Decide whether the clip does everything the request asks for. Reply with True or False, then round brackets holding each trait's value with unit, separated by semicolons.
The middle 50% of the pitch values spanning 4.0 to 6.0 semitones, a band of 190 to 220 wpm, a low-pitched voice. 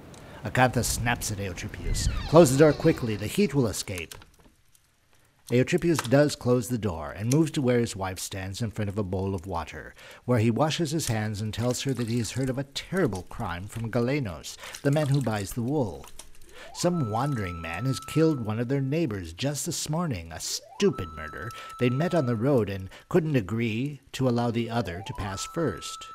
True (5.3 semitones; 195 wpm; 120 Hz)